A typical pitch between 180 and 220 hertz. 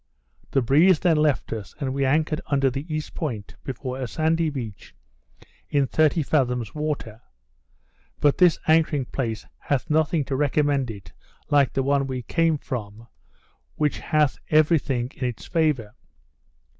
No: medium, 140 Hz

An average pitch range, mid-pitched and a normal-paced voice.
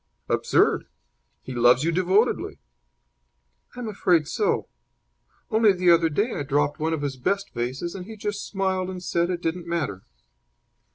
Yes: average, 5.0 semitones; medium, 175 Hz; average, 155 wpm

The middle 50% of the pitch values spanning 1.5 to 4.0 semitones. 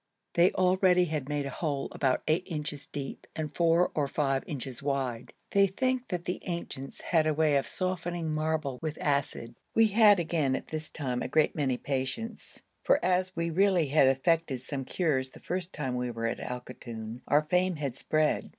No: average, 4.6 semitones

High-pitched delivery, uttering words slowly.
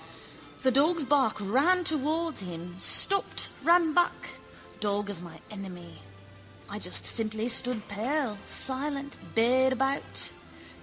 Yes: very high, 255 Hz; slow, 115 wpm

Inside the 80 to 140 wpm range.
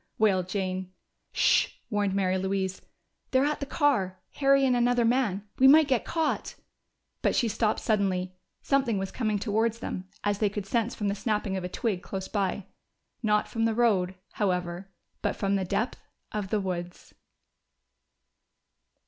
No: average, 160 wpm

